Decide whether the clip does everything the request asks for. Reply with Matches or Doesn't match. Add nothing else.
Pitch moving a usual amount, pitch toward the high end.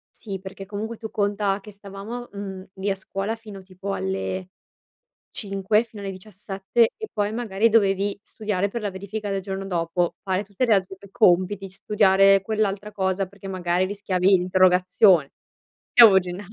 Doesn't match